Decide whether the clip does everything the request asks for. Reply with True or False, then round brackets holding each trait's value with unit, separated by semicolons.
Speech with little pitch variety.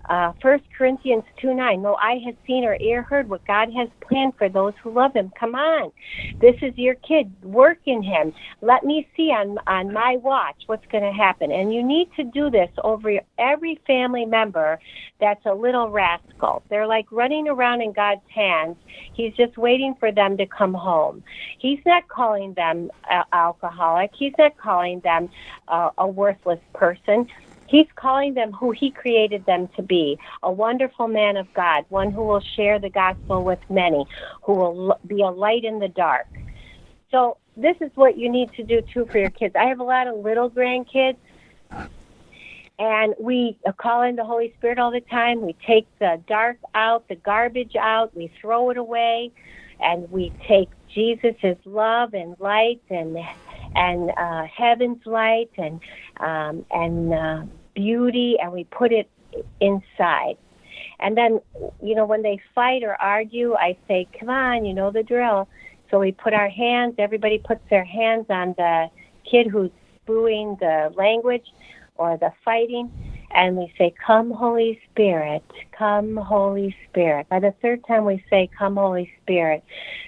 False (4.0 semitones)